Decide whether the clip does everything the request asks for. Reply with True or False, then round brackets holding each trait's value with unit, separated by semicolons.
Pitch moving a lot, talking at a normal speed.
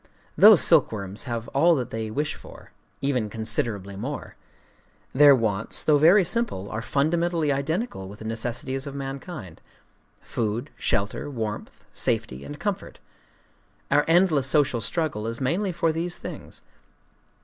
False (6.3 semitones; 125 wpm)